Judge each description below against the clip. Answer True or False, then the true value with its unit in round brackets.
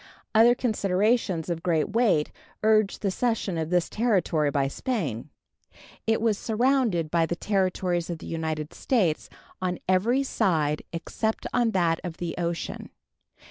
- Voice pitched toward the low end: False (185 Hz)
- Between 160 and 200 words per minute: False (140 wpm)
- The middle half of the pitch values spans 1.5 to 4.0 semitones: False (5.1 semitones)